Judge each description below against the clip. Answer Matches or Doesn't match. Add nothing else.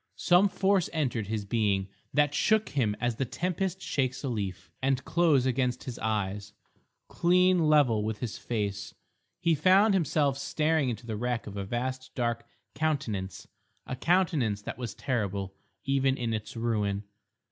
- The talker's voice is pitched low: Matches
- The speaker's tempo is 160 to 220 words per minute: Doesn't match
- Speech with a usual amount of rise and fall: Doesn't match